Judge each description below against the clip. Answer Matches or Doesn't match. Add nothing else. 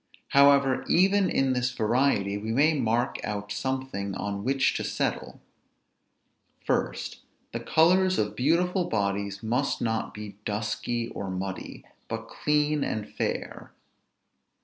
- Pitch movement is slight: Doesn't match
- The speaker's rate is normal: Doesn't match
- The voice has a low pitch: Matches